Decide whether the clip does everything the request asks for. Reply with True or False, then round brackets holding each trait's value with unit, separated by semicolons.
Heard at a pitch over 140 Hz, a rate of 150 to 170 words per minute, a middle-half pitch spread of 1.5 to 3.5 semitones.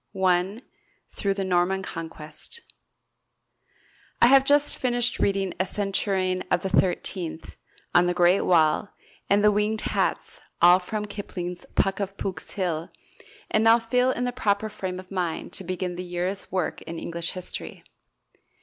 True (190 Hz; 155 wpm; 2.8 semitones)